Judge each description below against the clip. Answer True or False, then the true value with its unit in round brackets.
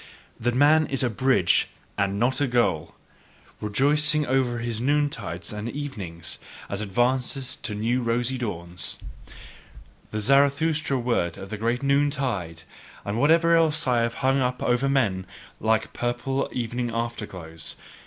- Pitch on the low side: True (120 Hz)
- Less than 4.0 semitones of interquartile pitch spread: False (4.5 semitones)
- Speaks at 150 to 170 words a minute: False (135 wpm)